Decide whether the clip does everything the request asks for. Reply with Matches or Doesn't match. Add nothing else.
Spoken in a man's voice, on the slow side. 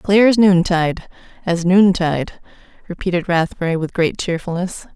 Doesn't match